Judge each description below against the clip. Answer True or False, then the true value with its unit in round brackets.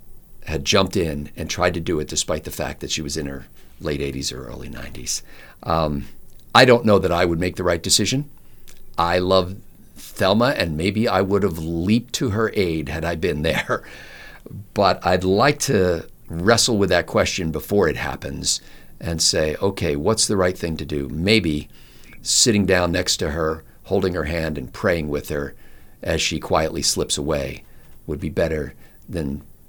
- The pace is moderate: True (180 wpm)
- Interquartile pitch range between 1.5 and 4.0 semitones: False (4.5 semitones)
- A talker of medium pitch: False (85 Hz)